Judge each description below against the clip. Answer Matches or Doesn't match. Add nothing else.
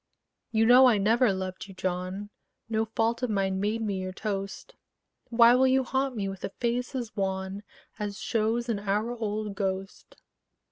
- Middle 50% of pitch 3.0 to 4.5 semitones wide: Matches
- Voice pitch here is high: Matches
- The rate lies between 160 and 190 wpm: Matches